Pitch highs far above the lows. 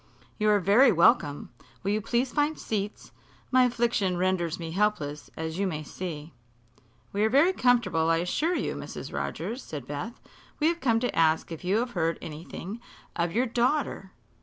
Yes: wide, 6.5 semitones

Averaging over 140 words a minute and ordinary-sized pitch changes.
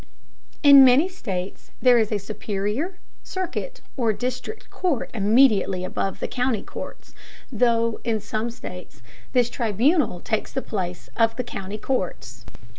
No: slow, 135 wpm; average, 4.6 semitones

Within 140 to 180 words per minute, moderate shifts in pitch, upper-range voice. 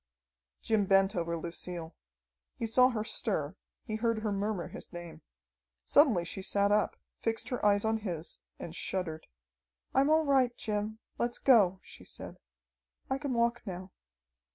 Yes: average, 155 wpm; average, 4.4 semitones; high, 210 Hz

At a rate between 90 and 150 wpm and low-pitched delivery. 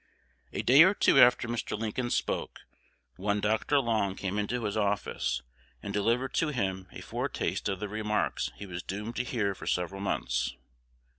No: average, 170 wpm; low, 105 Hz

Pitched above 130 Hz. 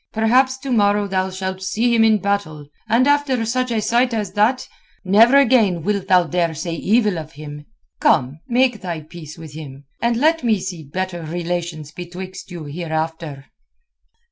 Yes: high, 190 Hz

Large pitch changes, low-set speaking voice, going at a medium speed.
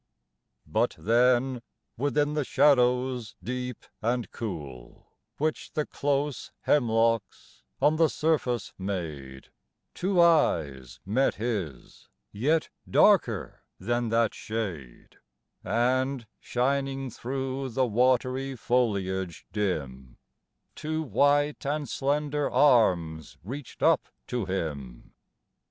No: wide, 6.0 semitones; low, 125 Hz; slow, 95 wpm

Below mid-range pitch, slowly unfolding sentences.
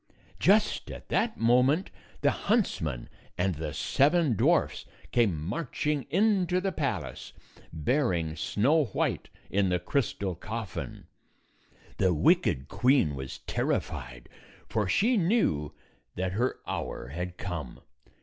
Yes: low, 110 Hz; slow, 120 wpm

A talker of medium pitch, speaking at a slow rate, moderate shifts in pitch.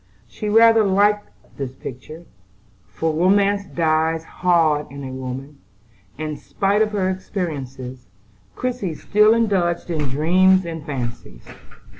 No: medium, 165 Hz; slow, 120 wpm; wide, 5.9 semitones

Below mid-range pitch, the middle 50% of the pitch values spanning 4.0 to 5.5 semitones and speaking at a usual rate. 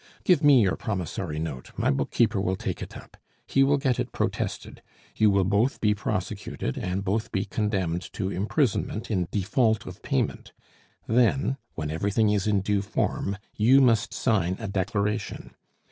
No: low, 100 Hz; average, 3.2 semitones; average, 160 wpm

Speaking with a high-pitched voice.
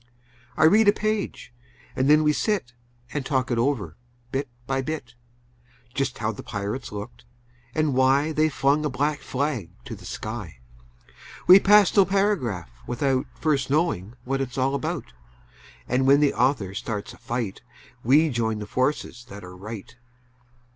No: low, 130 Hz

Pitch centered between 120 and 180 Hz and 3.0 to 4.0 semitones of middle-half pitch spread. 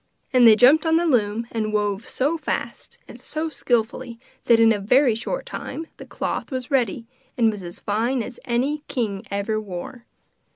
No: high, 235 Hz; average, 3.7 semitones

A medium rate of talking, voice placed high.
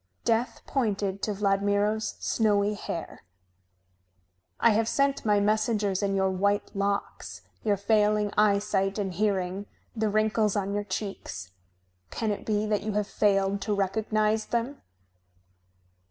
No: slow, 130 wpm; high, 205 Hz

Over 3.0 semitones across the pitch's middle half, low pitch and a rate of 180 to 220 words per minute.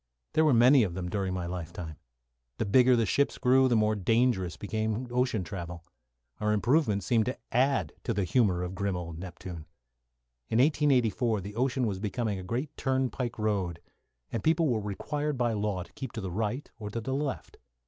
Yes: average, 5.1 semitones; low, 110 Hz; average, 190 wpm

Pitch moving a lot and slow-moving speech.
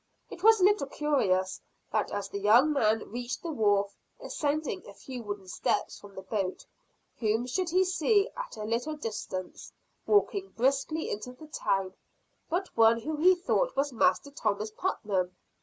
No: wide, 7.3 semitones; average, 165 wpm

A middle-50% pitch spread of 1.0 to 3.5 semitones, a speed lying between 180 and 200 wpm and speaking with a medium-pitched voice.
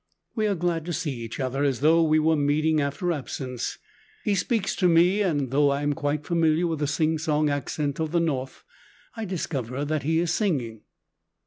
Yes: average, 3.0 semitones; average, 195 wpm; medium, 155 Hz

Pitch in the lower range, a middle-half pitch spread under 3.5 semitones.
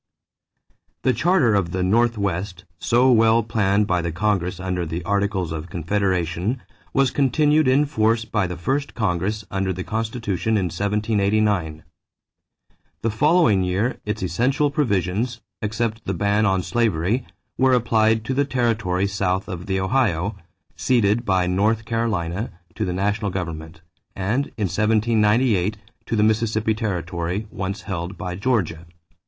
No: low, 105 Hz; average, 3.9 semitones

